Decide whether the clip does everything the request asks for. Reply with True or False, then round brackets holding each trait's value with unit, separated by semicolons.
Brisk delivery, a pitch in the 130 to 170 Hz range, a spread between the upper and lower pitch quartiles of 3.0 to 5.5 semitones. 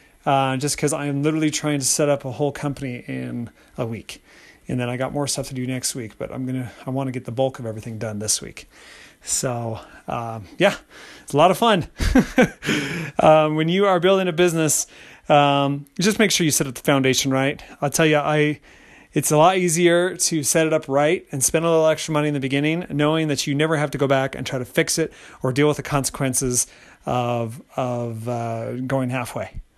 True (220 wpm; 140 Hz; 3.3 semitones)